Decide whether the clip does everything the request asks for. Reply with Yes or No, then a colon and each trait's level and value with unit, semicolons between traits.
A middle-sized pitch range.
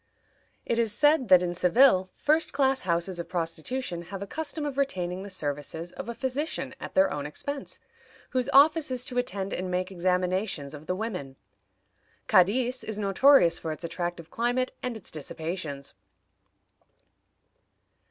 No: wide, 6.8 semitones